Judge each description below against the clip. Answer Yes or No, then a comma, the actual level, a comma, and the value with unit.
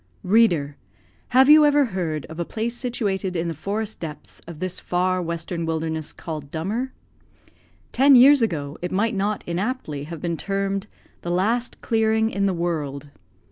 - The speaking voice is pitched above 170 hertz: Yes, medium, 185 Hz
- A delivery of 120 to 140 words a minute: No, average, 160 wpm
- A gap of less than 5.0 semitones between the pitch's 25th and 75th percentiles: No, wide, 5.4 semitones